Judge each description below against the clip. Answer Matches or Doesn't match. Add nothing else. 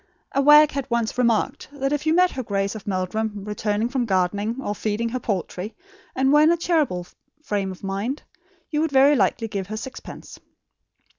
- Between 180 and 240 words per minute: Matches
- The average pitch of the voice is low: Doesn't match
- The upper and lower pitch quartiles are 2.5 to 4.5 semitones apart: Doesn't match